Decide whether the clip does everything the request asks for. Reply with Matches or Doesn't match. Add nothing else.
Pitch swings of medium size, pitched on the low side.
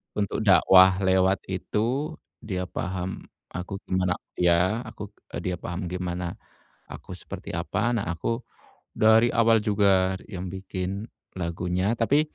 Matches